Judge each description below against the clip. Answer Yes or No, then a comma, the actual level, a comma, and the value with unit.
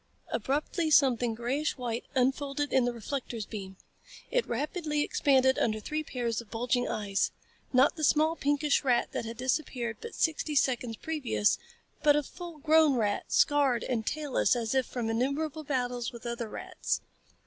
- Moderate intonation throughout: Yes, average, 4.0 semitones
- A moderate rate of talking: Yes, average, 160 wpm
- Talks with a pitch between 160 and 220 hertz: No, very high, 260 Hz